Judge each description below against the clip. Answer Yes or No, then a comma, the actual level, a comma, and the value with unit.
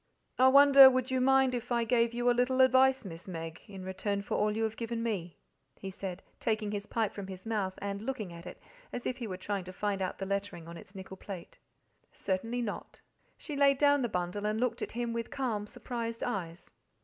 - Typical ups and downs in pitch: Yes, average, 4.3 semitones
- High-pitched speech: Yes, high, 220 Hz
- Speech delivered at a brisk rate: Yes, fast, 220 wpm